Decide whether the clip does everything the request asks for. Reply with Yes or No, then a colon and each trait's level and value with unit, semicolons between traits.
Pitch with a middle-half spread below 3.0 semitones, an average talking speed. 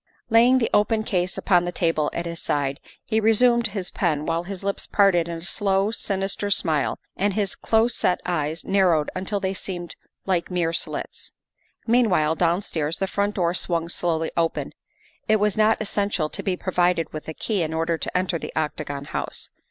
No: average, 3.7 semitones; average, 185 wpm